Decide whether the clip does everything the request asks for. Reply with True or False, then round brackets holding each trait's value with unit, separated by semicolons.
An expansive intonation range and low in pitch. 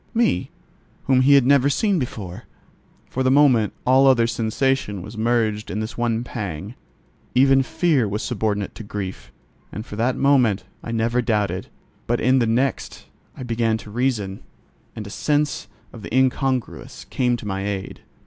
False (3.9 semitones; 115 Hz)